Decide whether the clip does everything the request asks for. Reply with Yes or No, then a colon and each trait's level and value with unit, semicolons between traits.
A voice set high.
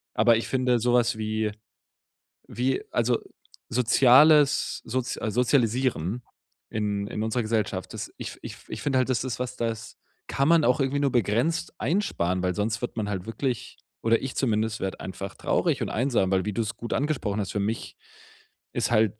No: low, 115 Hz